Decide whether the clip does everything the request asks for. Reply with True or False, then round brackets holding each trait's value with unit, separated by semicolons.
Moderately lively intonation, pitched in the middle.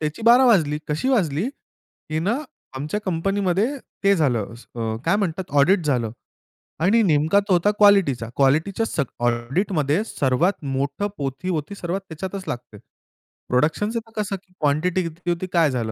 False (5.8 semitones; 165 Hz)